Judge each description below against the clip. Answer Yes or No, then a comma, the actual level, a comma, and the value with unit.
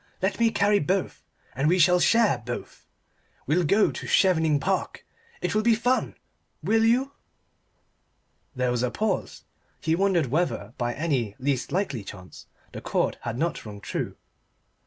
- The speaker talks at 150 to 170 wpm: Yes, average, 155 wpm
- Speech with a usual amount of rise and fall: No, wide, 8.2 semitones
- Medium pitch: Yes, medium, 170 Hz